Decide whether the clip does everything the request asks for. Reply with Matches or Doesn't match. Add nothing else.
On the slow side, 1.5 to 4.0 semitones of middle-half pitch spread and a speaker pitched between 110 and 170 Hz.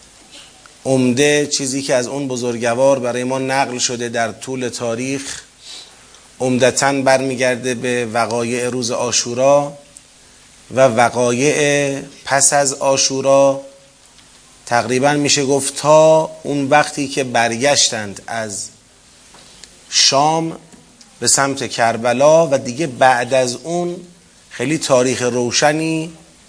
Matches